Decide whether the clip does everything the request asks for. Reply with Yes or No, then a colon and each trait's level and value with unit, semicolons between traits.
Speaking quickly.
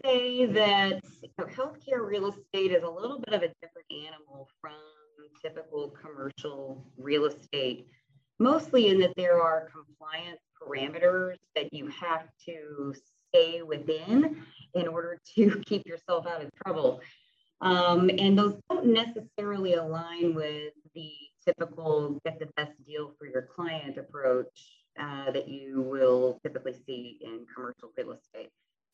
No: average, 140 wpm